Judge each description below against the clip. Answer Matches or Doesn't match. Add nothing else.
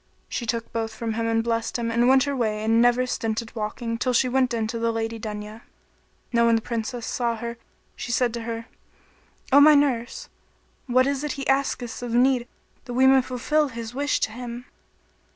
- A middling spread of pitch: Doesn't match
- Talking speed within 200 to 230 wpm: Matches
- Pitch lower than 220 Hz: Doesn't match